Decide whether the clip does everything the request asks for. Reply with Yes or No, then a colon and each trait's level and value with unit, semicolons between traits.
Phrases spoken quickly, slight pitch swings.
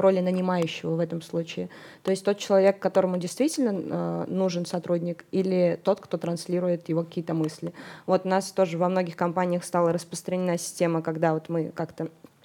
Yes: fast, 170 wpm; narrow, 1.9 semitones